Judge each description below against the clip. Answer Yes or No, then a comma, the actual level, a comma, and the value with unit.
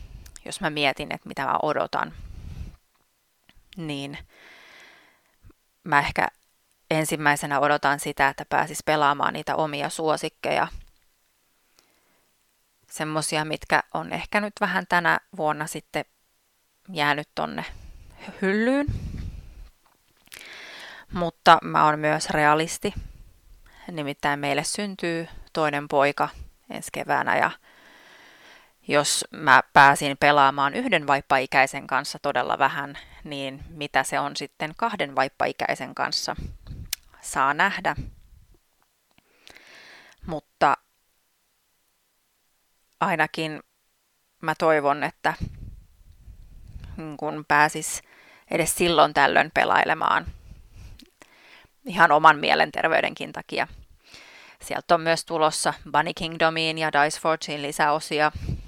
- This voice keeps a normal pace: No, slow, 90 wpm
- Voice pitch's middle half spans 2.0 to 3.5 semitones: Yes, average, 3.0 semitones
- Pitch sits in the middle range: Yes, medium, 150 Hz